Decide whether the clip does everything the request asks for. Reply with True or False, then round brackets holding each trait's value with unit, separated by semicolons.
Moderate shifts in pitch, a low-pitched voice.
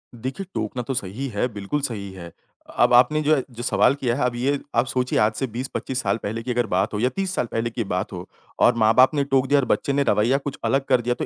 True (3.4 semitones; 125 Hz)